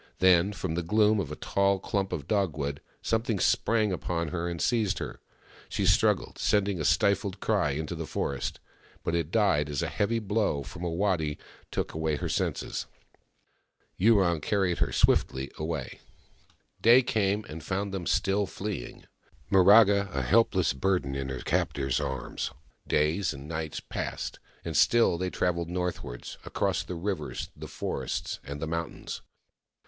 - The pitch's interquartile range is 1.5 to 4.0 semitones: No, average, 4.6 semitones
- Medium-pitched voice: No, very low, 90 Hz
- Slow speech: No, average, 155 wpm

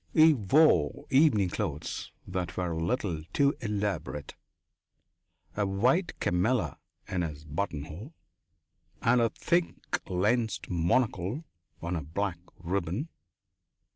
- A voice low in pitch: Yes, low, 100 Hz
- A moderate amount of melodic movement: No, wide, 6.5 semitones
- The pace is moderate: No, slow, 105 wpm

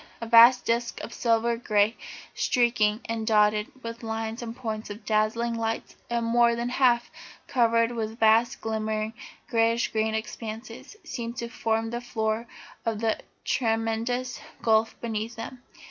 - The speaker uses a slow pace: No, average, 145 wpm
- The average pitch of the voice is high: Yes, high, 230 Hz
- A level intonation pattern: Yes, narrow, 1.2 semitones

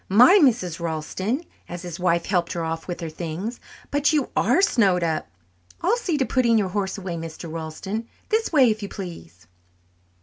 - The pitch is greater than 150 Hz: Yes, high, 190 Hz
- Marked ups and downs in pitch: Yes, wide, 6.5 semitones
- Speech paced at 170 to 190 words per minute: Yes, average, 180 wpm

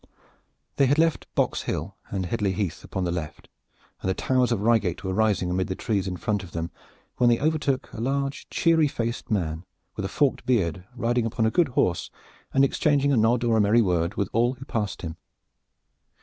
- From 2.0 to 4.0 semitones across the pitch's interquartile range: No, wide, 5.5 semitones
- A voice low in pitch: Yes, low, 110 Hz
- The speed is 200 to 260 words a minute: Yes, fast, 205 wpm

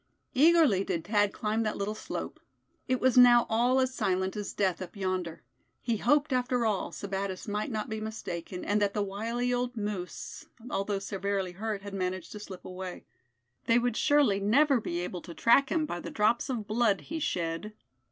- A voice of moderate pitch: No, high, 210 Hz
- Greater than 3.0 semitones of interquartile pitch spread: Yes, average, 3.9 semitones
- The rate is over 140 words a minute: Yes, average, 185 wpm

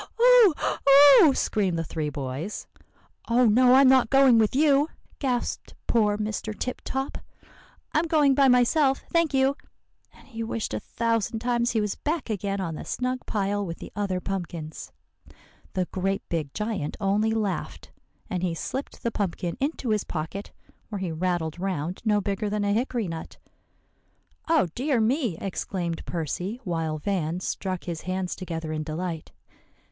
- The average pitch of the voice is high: Yes, high, 205 Hz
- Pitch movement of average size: No, wide, 6.1 semitones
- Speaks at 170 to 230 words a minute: No, average, 160 wpm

